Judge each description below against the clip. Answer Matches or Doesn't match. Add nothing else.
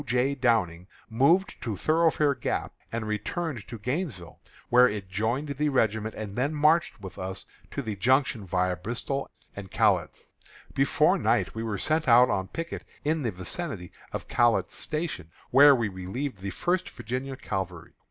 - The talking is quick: Doesn't match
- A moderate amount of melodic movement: Doesn't match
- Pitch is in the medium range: Doesn't match